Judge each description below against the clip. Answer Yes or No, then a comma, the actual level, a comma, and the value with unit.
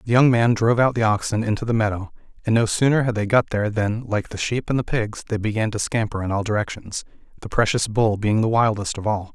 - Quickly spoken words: Yes, fast, 250 wpm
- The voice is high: No, low, 110 Hz